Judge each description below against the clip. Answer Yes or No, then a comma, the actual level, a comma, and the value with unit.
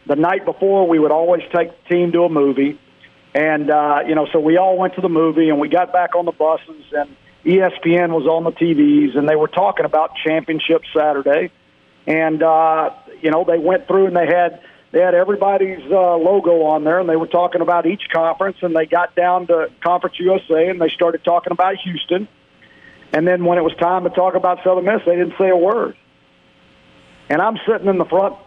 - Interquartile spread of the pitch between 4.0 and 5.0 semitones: No, narrow, 2.4 semitones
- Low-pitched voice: No, medium, 175 Hz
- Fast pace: Yes, fast, 215 wpm